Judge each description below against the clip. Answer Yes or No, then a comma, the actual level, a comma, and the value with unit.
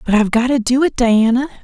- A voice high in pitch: Yes, high, 240 Hz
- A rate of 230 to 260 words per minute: Yes, fast, 255 wpm